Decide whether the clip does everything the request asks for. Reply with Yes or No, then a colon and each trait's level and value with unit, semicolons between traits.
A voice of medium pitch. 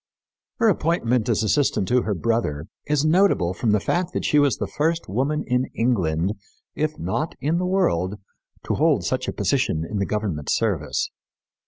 No: low, 120 Hz